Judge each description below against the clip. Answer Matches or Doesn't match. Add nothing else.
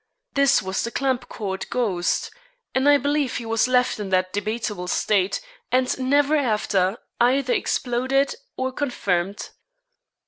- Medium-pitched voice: Doesn't match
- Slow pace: Matches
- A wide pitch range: Doesn't match